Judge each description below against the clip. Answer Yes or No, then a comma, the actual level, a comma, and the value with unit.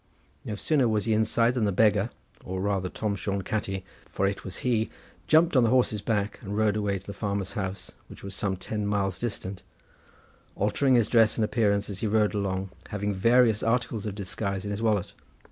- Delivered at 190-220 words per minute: Yes, average, 200 wpm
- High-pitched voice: No, low, 105 Hz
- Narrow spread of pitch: Yes, narrow, 2.2 semitones